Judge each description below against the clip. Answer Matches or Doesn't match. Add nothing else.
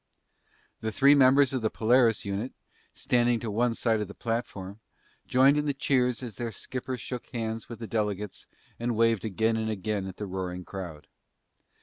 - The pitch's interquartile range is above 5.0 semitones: Doesn't match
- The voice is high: Doesn't match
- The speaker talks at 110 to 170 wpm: Doesn't match